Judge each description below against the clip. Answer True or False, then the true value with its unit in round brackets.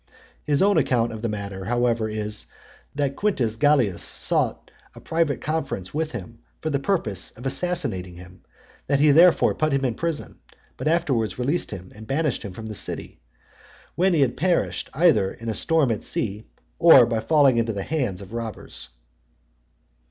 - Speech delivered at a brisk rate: False (165 wpm)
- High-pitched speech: False (125 Hz)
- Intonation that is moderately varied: False (6.4 semitones)